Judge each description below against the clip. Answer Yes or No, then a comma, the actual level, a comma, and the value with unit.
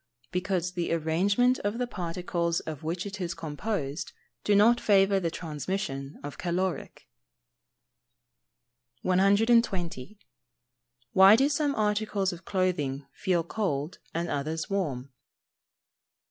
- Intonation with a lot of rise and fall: No, average, 3.9 semitones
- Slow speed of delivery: Yes, slow, 115 wpm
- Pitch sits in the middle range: Yes, medium, 180 Hz